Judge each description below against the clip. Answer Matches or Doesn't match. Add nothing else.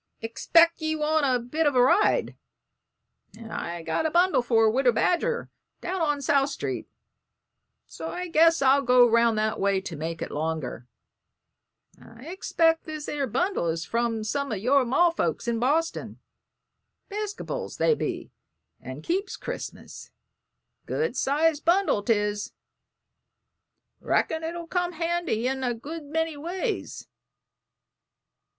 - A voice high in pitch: Matches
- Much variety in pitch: Matches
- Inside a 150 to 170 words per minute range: Doesn't match